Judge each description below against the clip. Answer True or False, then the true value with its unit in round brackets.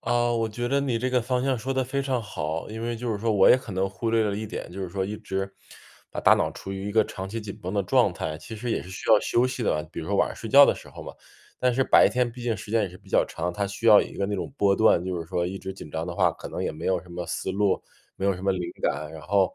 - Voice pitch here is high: False (105 Hz)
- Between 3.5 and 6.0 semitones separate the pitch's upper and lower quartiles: True (3.9 semitones)